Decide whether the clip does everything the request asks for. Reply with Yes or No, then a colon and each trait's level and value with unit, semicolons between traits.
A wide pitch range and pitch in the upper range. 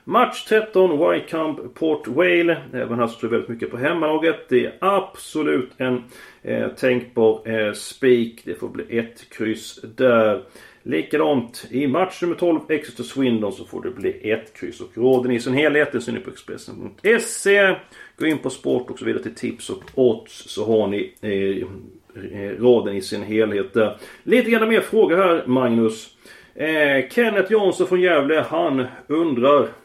No: wide, 7.8 semitones; low, 135 Hz